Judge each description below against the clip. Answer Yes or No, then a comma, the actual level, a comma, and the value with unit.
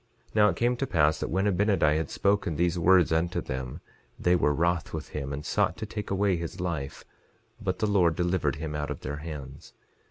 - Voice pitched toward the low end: Yes, very low, 85 Hz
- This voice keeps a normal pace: No, fast, 215 wpm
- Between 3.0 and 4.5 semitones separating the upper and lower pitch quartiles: Yes, average, 4.2 semitones